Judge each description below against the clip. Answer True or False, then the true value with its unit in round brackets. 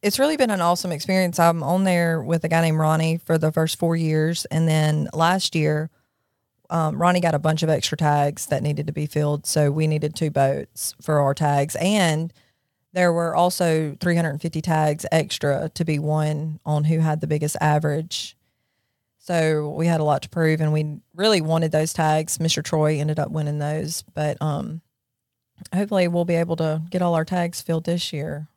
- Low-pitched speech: False (155 Hz)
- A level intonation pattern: True (2.0 semitones)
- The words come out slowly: False (195 wpm)